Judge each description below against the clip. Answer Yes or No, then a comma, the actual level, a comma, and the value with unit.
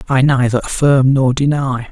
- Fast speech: No, average, 155 wpm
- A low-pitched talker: Yes, low, 130 Hz